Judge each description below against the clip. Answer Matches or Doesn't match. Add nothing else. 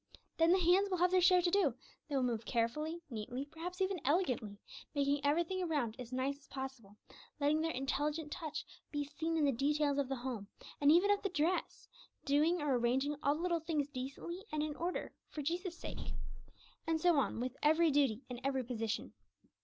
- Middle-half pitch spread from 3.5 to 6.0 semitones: Matches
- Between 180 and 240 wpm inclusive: Matches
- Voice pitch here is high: Matches